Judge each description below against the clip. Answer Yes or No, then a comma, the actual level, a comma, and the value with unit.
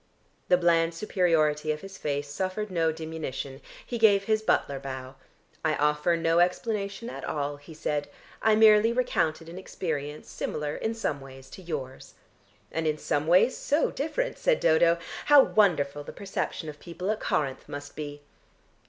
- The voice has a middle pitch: Yes, medium, 165 Hz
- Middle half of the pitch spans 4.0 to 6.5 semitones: Yes, average, 5.2 semitones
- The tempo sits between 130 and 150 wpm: No, average, 160 wpm